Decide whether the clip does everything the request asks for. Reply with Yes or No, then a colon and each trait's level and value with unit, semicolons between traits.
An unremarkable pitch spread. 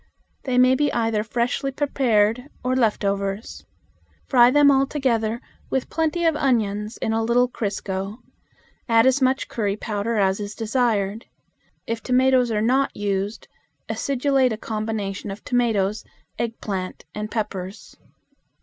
Yes: average, 3.6 semitones